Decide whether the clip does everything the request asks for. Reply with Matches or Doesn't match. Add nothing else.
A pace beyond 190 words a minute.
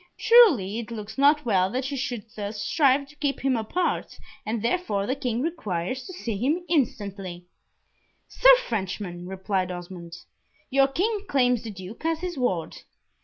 Doesn't match